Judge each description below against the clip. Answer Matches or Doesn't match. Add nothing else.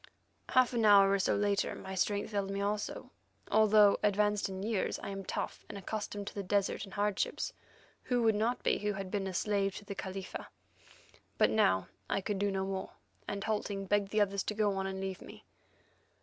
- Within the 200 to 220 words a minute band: Matches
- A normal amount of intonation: Doesn't match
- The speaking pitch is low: Doesn't match